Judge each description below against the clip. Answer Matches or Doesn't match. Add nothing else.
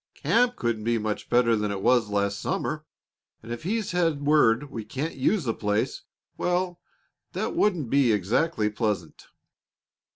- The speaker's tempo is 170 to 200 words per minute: Doesn't match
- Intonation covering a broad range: Matches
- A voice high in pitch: Doesn't match